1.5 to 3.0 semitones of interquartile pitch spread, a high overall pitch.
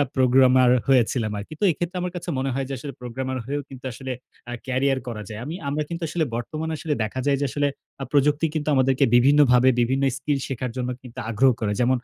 No: narrow, 2.6 semitones; low, 130 Hz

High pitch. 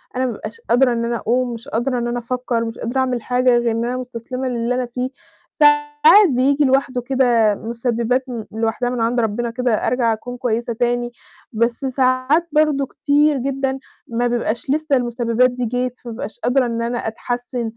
Yes: high, 245 Hz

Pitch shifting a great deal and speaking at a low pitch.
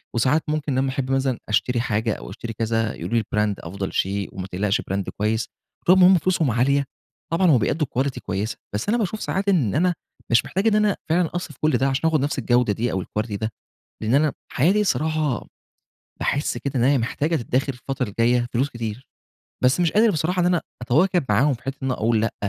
Yes: wide, 5.8 semitones; low, 130 Hz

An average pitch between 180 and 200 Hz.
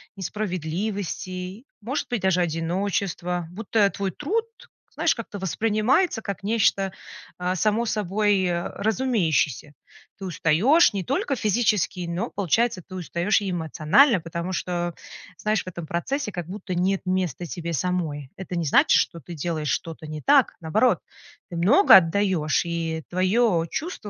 Yes: medium, 185 Hz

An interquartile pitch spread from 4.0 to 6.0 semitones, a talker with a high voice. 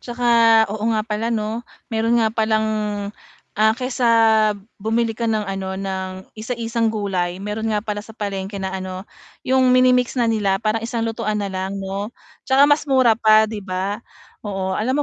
No: average, 2.9 semitones; high, 215 Hz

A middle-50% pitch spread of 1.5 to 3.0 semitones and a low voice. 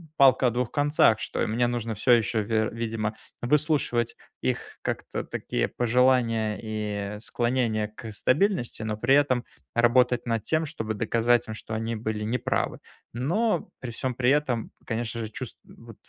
Yes: narrow, 2.5 semitones; low, 120 Hz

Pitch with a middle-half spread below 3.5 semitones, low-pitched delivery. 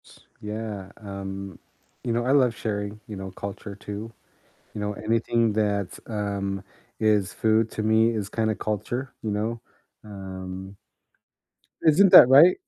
Yes: narrow, 2.4 semitones; low, 105 Hz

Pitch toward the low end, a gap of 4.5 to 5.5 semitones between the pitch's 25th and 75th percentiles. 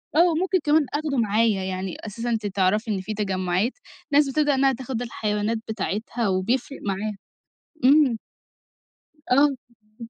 No: high, 230 Hz; average, 4.8 semitones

